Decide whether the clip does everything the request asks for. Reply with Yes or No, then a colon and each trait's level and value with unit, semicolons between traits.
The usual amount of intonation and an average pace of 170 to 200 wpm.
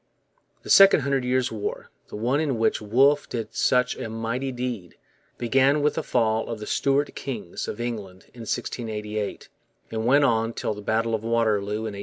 Yes: average, 3.2 semitones; average, 185 wpm